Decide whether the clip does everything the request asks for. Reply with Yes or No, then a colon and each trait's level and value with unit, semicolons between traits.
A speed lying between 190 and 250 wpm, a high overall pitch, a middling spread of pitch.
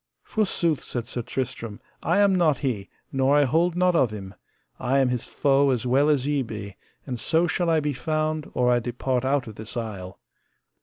No: average, 200 wpm; low, 135 Hz; average, 4.3 semitones